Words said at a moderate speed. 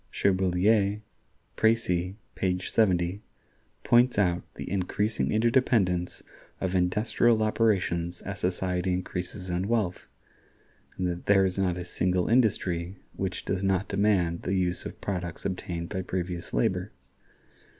No: slow, 125 wpm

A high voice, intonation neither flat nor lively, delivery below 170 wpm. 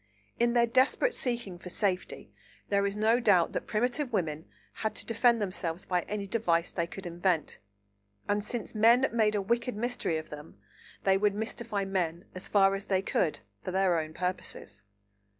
No: high, 200 Hz; average, 4.2 semitones; average, 175 wpm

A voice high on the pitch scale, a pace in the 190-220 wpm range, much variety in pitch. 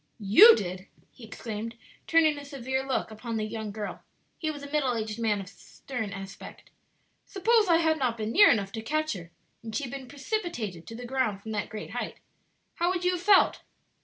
Yes: high, 245 Hz; fast, 205 wpm; wide, 6.3 semitones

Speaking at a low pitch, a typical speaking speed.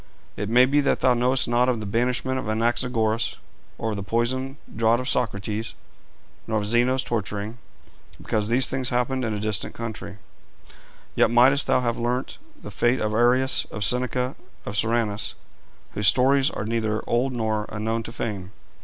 Yes: low, 115 Hz; average, 160 wpm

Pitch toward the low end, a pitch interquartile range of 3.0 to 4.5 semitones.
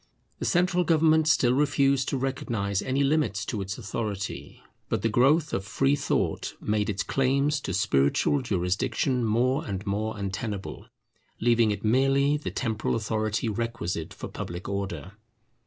No: low, 115 Hz; average, 5.3 semitones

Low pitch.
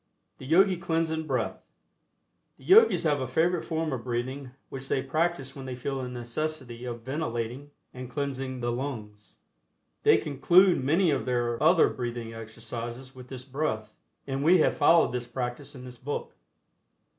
Yes: low, 130 Hz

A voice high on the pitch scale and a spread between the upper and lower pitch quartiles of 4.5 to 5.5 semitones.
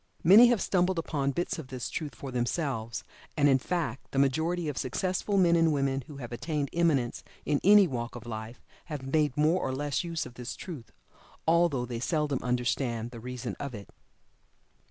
No: medium, 140 Hz; average, 5.0 semitones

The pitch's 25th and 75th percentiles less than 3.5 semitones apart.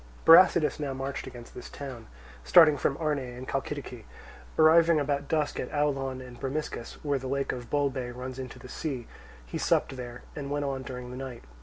Yes: narrow, 2.5 semitones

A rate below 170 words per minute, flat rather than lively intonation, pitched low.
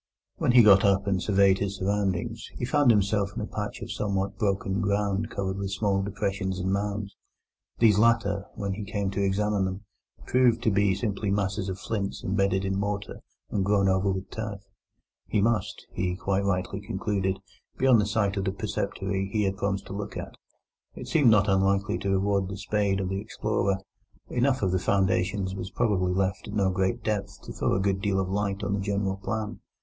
No: average, 200 wpm; narrow, 1.3 semitones; low, 100 Hz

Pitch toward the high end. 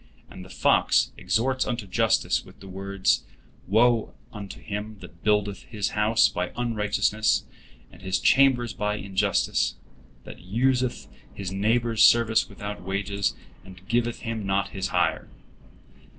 No: low, 105 Hz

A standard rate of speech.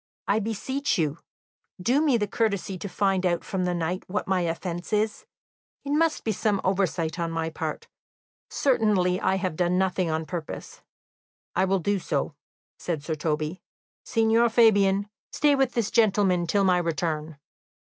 Yes: average, 160 wpm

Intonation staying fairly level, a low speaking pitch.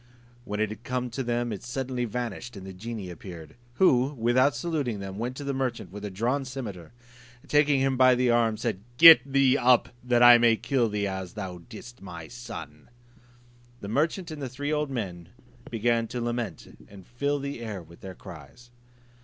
No: average, 4.3 semitones; low, 120 Hz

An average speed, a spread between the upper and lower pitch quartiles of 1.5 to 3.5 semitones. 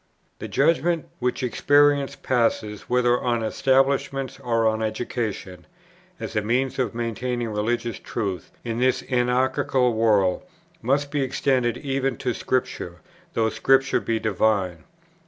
No: slow, 125 wpm; average, 3.2 semitones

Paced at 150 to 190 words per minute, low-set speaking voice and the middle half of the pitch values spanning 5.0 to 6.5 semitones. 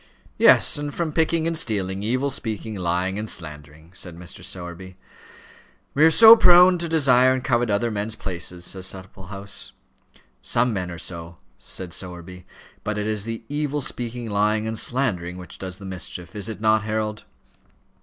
Yes: average, 165 wpm; low, 105 Hz; average, 5.3 semitones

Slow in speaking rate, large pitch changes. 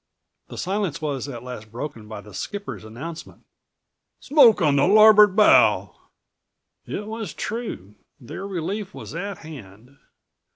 Yes: slow, 130 wpm; wide, 8.8 semitones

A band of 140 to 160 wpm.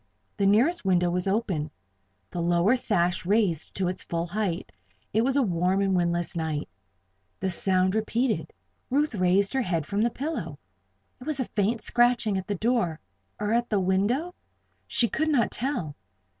No: average, 170 wpm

